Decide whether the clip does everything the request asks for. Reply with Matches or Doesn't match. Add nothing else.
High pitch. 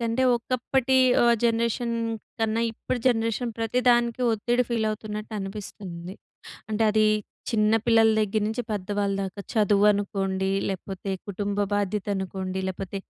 Matches